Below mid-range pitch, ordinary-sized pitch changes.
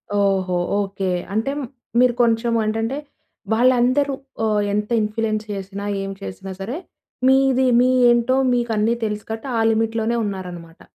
No: high, 220 Hz; average, 3.2 semitones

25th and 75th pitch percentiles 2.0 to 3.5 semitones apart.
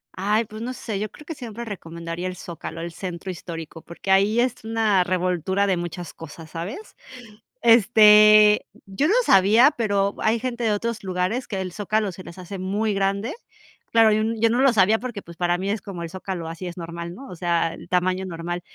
No: average, 3.9 semitones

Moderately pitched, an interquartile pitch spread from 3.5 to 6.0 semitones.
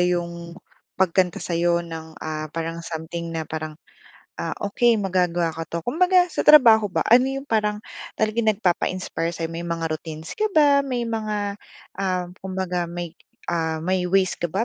Yes: medium, 180 Hz; average, 4.2 semitones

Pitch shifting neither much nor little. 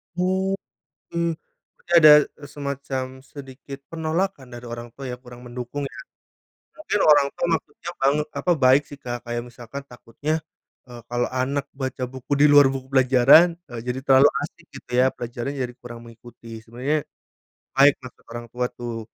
Yes: average, 3.0 semitones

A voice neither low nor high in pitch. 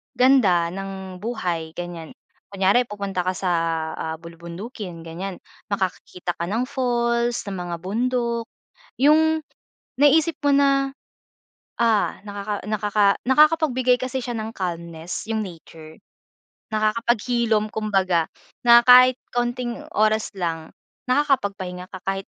No: high, 215 Hz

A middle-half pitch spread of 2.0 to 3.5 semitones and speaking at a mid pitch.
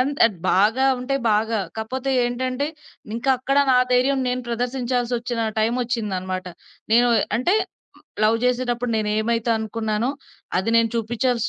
No: narrow, 2.4 semitones; high, 240 Hz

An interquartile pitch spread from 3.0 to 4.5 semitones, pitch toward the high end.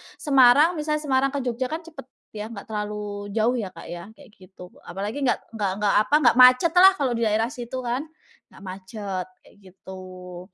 No: wide, 5.4 semitones; high, 230 Hz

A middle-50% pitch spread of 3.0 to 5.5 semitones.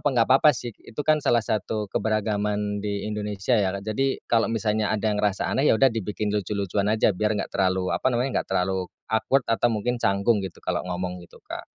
No: narrow, 2.5 semitones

